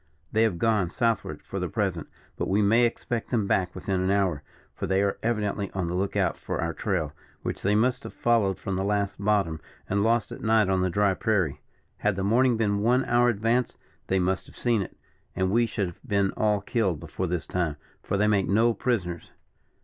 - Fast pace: Yes, fast, 215 wpm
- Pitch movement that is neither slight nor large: Yes, average, 3.1 semitones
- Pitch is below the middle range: Yes, low, 100 Hz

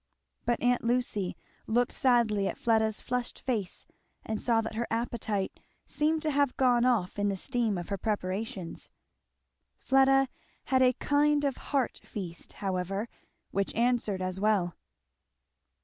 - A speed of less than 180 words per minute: Yes, average, 140 wpm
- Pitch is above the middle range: Yes, high, 230 Hz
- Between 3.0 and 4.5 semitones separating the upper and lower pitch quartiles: Yes, average, 4.1 semitones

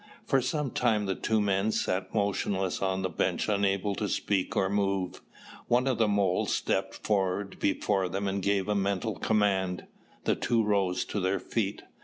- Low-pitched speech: Yes, low, 100 Hz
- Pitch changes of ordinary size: No, narrow, 1.7 semitones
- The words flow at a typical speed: Yes, average, 170 wpm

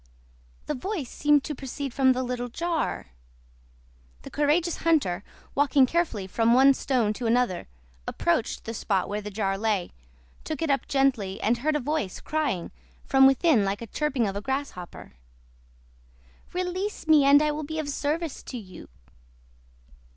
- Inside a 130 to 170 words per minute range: Yes, average, 160 wpm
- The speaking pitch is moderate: No, very high, 270 Hz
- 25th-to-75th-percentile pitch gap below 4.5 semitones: No, wide, 5.4 semitones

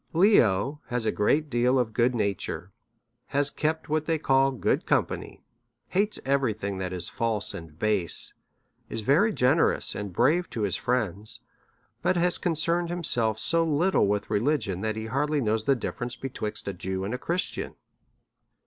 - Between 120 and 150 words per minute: No, average, 165 wpm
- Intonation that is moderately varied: No, wide, 6.7 semitones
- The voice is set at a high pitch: No, low, 125 Hz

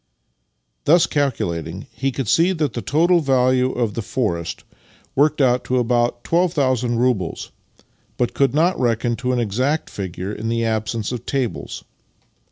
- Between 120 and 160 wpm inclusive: Yes, average, 150 wpm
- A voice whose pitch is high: No, low, 125 Hz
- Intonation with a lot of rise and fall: No, average, 3.5 semitones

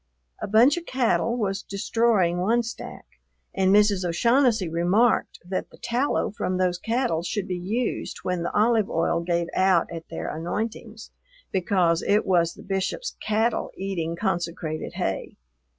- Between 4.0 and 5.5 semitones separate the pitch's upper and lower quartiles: Yes, average, 4.6 semitones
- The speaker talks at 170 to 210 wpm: No, average, 150 wpm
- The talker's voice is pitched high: Yes, high, 195 Hz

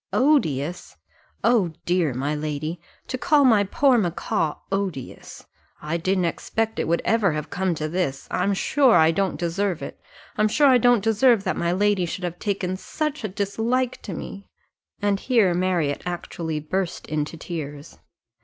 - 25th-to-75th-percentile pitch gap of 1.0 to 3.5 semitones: No, average, 4.8 semitones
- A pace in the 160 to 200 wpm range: Yes, average, 165 wpm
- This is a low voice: No, medium, 185 Hz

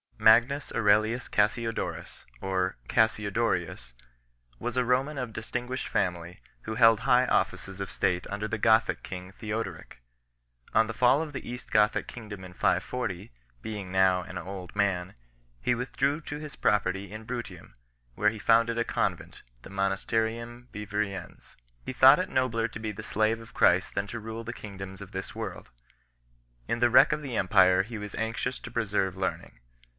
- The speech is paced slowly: No, average, 170 wpm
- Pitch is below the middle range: Yes, low, 110 Hz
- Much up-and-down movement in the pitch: No, average, 3.5 semitones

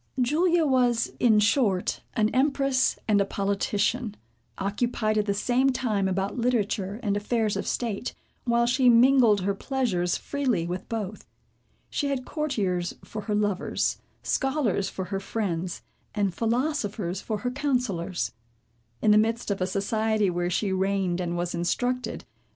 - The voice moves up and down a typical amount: Yes, average, 4.2 semitones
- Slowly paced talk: No, average, 145 wpm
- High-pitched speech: Yes, high, 215 Hz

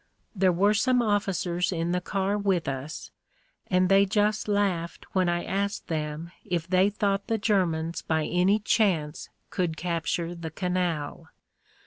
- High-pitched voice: No, medium, 180 Hz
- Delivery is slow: No, average, 150 wpm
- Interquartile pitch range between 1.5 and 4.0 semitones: Yes, average, 3.1 semitones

